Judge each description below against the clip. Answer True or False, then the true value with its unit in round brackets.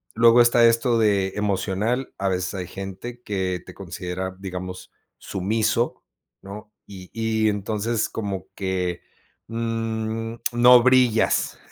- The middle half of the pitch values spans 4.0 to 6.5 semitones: False (3.4 semitones)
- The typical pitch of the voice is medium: False (105 Hz)